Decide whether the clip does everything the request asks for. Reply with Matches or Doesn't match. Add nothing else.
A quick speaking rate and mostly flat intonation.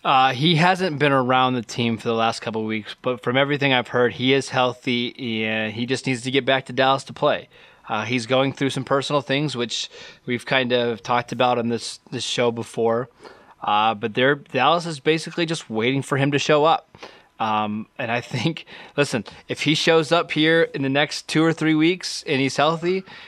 Doesn't match